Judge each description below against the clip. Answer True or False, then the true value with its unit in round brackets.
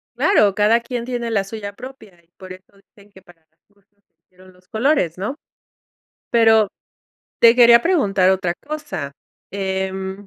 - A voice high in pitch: True (200 Hz)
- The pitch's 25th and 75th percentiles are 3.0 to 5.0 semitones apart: True (3.8 semitones)